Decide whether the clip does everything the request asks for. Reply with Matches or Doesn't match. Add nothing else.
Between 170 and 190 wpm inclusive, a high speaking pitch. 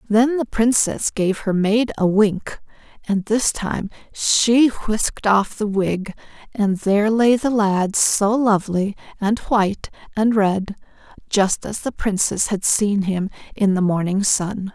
Doesn't match